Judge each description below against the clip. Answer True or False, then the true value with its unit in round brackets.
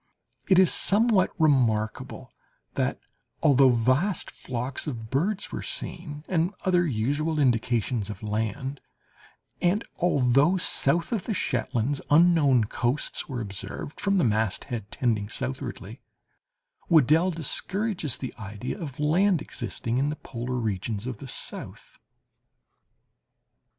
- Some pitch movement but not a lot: False (6.3 semitones)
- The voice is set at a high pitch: False (135 Hz)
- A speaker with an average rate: False (120 wpm)